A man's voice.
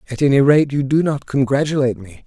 Yes: male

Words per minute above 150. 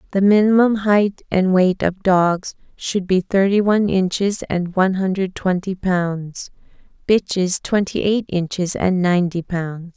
No: average, 145 wpm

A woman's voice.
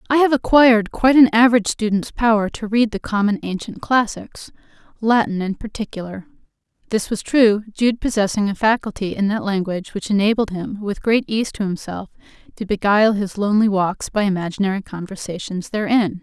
Yes: female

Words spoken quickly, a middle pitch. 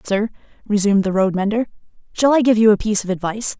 No: fast, 215 wpm; high, 210 Hz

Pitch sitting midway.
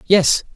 Yes: medium, 175 Hz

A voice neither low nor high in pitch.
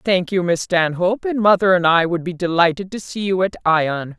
Yes: medium, 180 Hz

